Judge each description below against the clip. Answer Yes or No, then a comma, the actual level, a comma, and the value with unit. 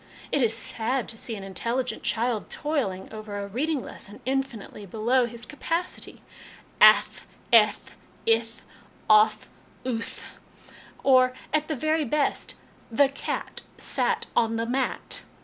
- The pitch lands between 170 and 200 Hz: No, high, 235 Hz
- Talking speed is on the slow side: Yes, slow, 130 wpm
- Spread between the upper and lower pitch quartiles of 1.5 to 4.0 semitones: Yes, average, 3.7 semitones